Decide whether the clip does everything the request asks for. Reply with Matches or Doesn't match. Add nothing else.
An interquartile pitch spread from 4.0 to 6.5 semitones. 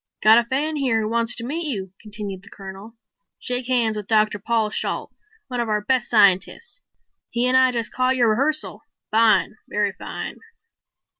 Doesn't match